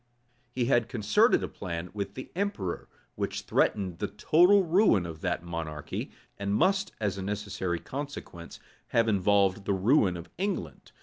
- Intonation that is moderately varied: No, wide, 6.3 semitones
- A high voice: No, low, 100 Hz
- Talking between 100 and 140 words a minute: No, average, 150 wpm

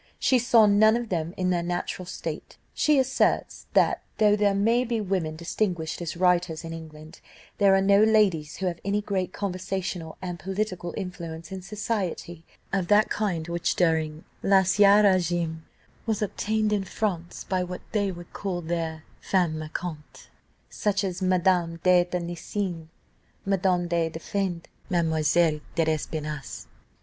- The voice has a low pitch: No, medium, 180 Hz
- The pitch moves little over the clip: No, average, 3.2 semitones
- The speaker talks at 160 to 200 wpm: No, average, 145 wpm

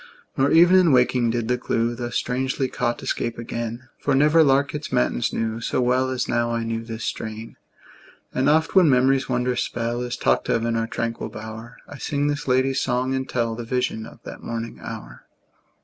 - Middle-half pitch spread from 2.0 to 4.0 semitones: Yes, narrow, 2.4 semitones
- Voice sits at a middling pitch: No, low, 125 Hz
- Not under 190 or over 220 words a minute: Yes, average, 195 wpm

